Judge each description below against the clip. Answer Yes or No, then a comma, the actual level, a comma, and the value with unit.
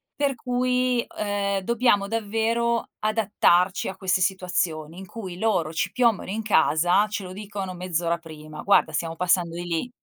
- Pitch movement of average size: Yes, average, 4.2 semitones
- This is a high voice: Yes, high, 195 Hz